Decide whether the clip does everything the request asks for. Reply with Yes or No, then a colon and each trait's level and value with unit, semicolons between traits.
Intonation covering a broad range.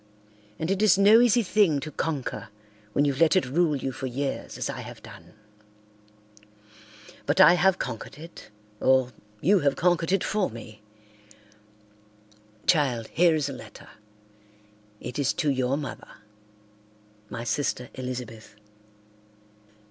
Yes: wide, 6.5 semitones